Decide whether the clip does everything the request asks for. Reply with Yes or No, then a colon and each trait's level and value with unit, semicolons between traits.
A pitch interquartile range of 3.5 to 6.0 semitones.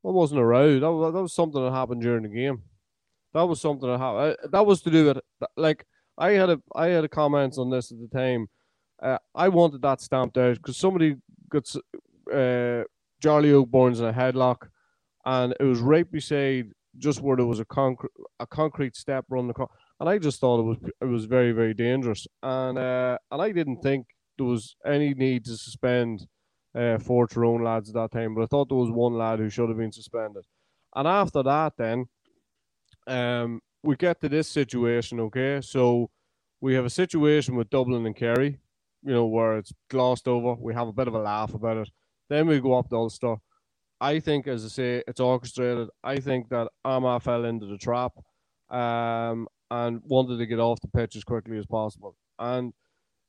No: average, 3.1 semitones